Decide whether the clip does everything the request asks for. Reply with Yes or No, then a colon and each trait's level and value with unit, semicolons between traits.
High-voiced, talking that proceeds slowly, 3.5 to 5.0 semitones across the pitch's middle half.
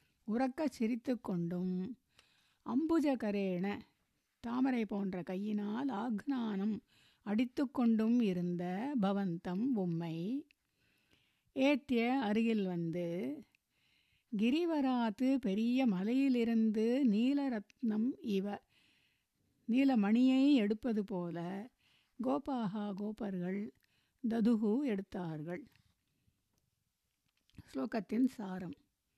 Yes: high, 225 Hz; slow, 60 wpm; average, 4.5 semitones